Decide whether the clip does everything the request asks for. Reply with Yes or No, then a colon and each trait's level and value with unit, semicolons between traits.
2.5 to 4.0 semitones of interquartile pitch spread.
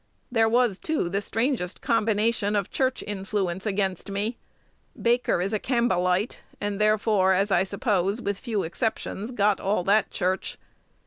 Yes: average, 2.8 semitones